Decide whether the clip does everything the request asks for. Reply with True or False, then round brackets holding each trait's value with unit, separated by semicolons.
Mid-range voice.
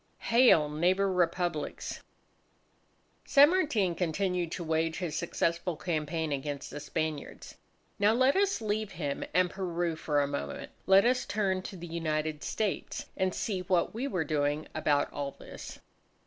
True (175 Hz)